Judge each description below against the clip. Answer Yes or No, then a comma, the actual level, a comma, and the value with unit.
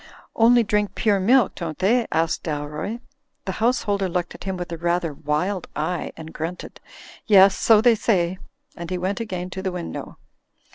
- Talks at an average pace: Yes, average, 180 wpm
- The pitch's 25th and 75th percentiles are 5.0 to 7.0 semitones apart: No, average, 3.5 semitones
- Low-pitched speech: No, medium, 185 Hz